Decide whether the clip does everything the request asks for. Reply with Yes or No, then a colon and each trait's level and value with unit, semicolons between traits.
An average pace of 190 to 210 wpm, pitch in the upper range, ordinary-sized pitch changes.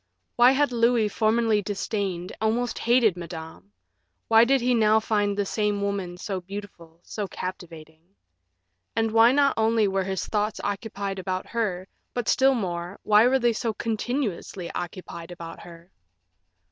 No: average, 145 wpm; high, 205 Hz; average, 3.9 semitones